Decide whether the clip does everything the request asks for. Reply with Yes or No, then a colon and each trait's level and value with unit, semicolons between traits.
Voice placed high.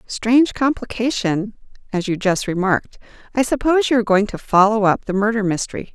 Yes: high, 215 Hz